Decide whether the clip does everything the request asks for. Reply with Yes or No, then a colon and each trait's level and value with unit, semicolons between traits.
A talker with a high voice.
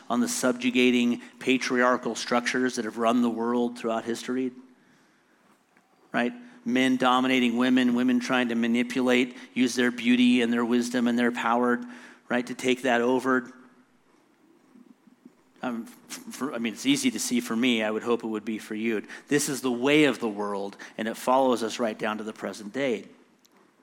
No: low, 125 Hz